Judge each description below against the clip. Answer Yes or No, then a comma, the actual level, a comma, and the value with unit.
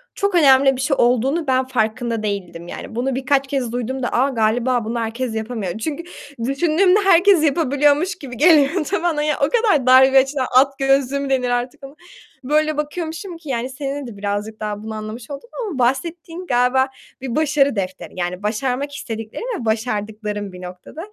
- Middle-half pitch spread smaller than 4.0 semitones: No, average, 4.7 semitones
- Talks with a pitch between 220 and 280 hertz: Yes, very high, 260 Hz